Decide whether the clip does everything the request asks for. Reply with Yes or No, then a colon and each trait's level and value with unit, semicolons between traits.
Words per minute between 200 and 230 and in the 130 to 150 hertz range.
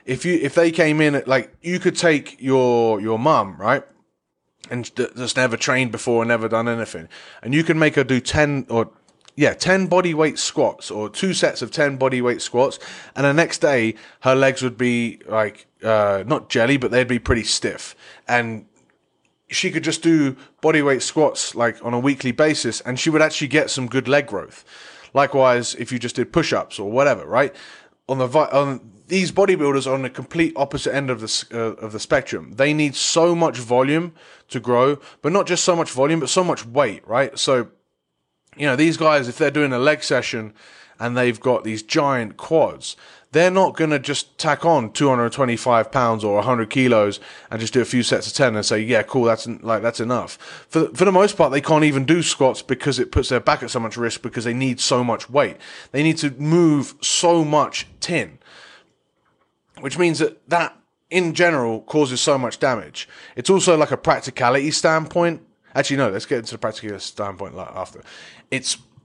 Yes: fast, 205 wpm; low, 135 Hz